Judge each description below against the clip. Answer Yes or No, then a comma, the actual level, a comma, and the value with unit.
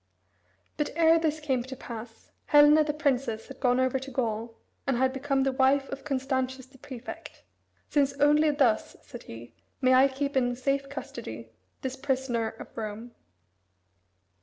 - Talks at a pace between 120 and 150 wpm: No, average, 160 wpm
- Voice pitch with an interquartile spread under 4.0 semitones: Yes, narrow, 2.4 semitones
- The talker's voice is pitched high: Yes, very high, 265 Hz